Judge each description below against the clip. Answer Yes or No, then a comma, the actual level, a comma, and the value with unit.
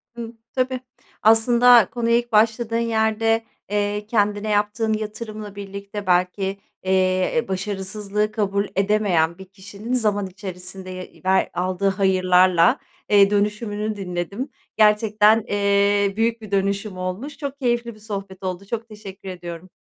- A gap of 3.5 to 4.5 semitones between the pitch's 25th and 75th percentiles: No, narrow, 2.5 semitones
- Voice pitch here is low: No, high, 205 Hz